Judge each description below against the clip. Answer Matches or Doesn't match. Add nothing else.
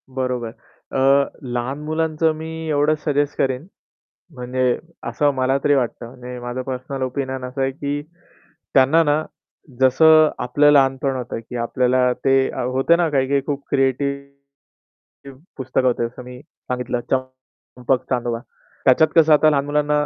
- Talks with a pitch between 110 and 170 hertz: Matches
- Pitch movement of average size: Doesn't match